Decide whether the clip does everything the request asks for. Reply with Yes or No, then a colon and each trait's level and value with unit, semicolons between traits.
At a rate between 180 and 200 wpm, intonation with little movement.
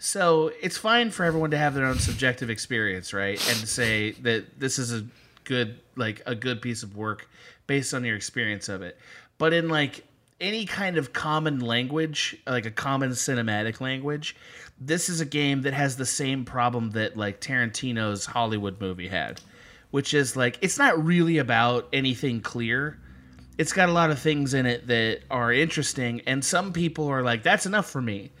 No: average, 185 wpm; average, 4.6 semitones